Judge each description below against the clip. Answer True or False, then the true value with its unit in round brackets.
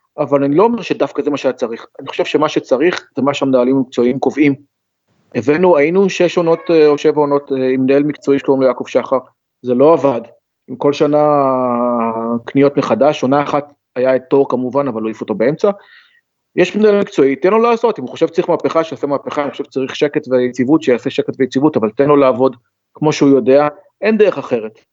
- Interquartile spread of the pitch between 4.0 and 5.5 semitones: False (2.9 semitones)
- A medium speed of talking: False (190 wpm)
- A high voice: False (140 Hz)